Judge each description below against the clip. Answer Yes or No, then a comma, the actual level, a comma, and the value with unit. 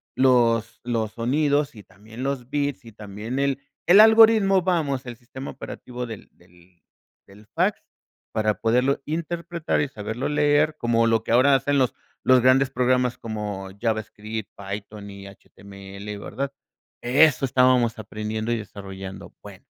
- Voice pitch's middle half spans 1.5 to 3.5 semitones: No, average, 4.6 semitones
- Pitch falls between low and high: No, low, 120 Hz